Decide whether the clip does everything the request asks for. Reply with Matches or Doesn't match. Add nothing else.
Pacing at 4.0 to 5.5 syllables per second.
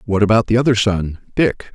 Doesn't match